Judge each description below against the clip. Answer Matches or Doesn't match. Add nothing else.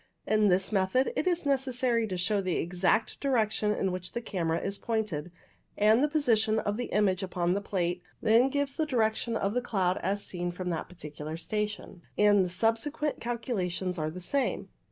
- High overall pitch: Matches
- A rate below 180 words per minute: Doesn't match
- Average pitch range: Matches